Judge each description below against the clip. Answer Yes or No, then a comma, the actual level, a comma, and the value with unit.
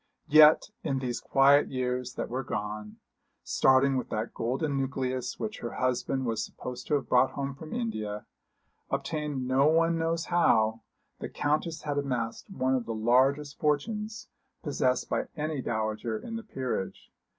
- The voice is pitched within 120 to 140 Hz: Yes, low, 135 Hz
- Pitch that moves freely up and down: No, average, 3.5 semitones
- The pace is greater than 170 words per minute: No, average, 155 wpm